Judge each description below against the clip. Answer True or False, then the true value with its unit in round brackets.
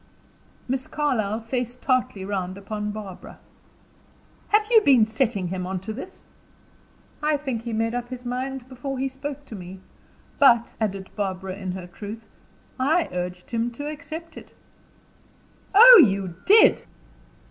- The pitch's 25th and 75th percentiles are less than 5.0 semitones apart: False (5.4 semitones)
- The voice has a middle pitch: False (235 Hz)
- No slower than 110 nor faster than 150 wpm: True (145 wpm)